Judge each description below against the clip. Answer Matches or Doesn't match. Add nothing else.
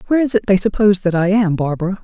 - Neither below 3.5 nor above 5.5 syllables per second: Doesn't match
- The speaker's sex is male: Doesn't match